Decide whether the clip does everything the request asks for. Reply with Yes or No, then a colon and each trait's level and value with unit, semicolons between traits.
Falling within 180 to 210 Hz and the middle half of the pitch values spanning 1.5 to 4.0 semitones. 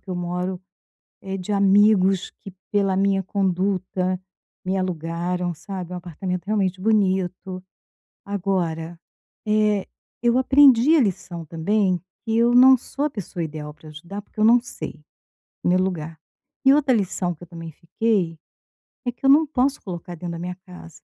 Yes: high, 190 Hz; average, 3.3 semitones